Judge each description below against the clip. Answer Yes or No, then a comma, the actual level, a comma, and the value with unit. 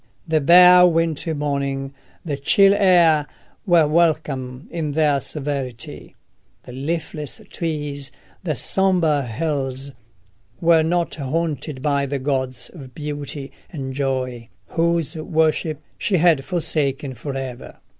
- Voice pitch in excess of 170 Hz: No, medium, 150 Hz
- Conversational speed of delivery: No, slow, 115 wpm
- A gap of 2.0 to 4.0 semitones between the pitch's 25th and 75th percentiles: Yes, average, 3.3 semitones